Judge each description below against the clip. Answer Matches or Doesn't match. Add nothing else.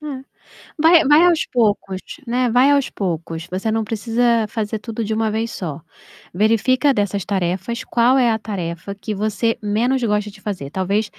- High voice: Matches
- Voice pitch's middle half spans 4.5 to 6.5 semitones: Doesn't match